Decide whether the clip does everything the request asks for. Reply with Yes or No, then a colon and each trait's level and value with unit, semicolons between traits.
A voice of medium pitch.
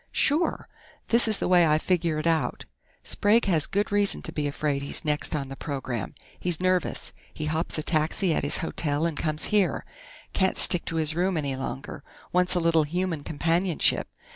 Yes: medium, 165 Hz